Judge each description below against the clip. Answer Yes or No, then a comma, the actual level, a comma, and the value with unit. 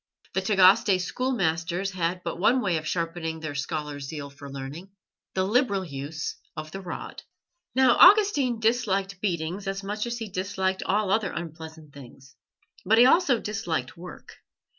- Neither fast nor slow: Yes, average, 155 wpm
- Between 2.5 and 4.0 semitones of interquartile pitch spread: No, average, 4.9 semitones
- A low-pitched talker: No, medium, 185 Hz